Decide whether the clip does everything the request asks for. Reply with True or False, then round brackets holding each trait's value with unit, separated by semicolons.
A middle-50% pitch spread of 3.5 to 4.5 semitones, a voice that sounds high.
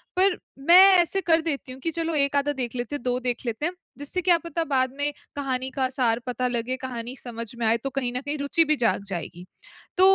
True (3.8 semitones; 270 Hz)